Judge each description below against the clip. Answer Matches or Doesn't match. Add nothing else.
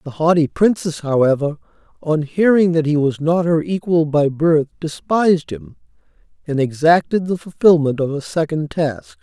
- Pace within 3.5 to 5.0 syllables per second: Matches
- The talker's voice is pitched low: Doesn't match